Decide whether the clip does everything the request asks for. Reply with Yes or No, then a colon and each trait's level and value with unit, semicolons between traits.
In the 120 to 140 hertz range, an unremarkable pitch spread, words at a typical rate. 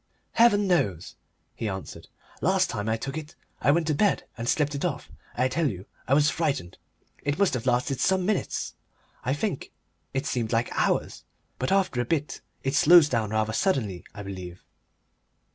No: low, 135 Hz; wide, 6.6 semitones; average, 180 wpm